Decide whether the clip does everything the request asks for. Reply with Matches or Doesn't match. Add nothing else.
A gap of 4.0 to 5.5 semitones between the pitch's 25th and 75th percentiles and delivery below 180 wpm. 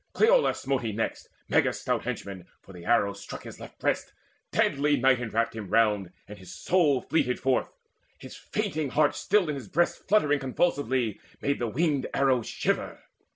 Matches